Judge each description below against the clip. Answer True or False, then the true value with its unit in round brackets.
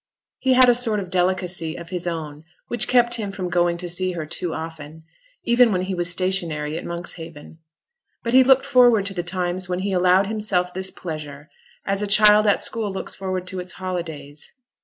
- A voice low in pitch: False (185 Hz)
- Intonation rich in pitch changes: False (3.1 semitones)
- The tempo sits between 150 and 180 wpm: False (200 wpm)